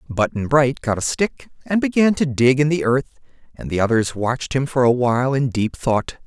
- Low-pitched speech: Yes, low, 130 Hz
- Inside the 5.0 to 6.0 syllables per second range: Yes, 5.2 syllables/s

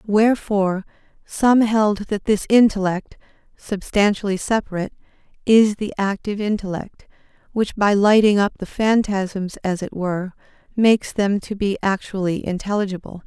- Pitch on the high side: Yes, high, 200 Hz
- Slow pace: Yes, slow, 120 wpm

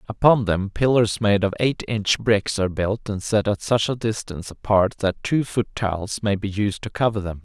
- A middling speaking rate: No, fast, 220 wpm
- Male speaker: Yes, male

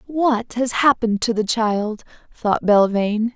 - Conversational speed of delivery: Yes, average, 145 wpm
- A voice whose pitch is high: Yes, high, 225 Hz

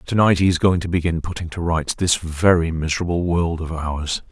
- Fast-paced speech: Yes, fast, 210 wpm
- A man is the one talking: Yes, male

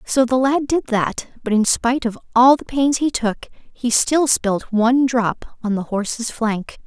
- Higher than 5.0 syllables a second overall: No, 4.1 syllables/s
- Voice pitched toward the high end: Yes, high, 240 Hz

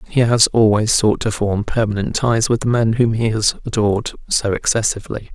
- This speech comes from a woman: No, male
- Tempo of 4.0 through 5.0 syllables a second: No, 5.3 syllables/s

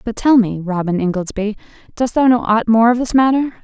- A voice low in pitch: No, high, 225 Hz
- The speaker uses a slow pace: No, average, 200 wpm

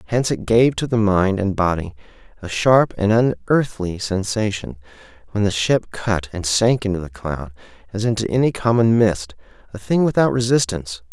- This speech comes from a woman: No, male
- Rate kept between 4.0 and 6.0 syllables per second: Yes, 5.0 syllables/s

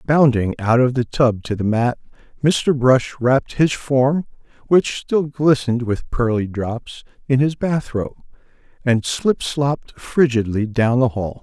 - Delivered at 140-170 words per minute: Yes, average, 160 wpm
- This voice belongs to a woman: No, male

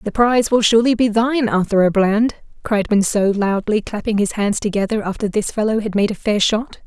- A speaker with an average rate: No, fast, 210 wpm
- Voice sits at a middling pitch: No, high, 215 Hz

